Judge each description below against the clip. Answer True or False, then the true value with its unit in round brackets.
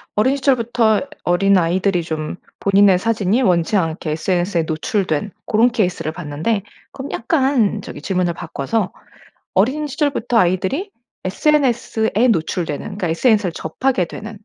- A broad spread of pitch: False (5.0 semitones)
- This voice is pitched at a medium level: False (200 Hz)